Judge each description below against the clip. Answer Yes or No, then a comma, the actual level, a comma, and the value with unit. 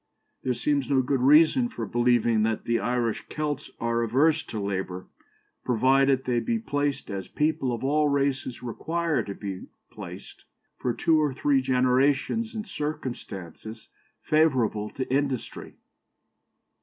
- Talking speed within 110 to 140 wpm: Yes, slow, 135 wpm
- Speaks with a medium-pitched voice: No, low, 130 Hz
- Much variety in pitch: No, average, 4.0 semitones